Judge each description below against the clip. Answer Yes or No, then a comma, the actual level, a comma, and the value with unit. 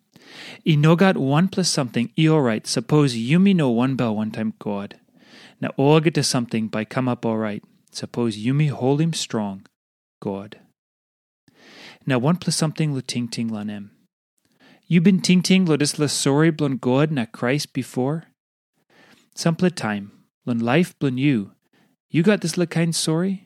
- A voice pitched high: No, medium, 140 Hz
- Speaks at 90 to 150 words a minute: No, average, 175 wpm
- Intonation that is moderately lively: No, wide, 5.9 semitones